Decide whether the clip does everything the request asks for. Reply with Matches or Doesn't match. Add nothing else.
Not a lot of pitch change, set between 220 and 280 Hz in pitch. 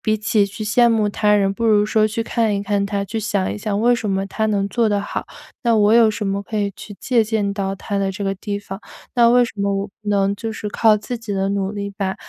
Doesn't match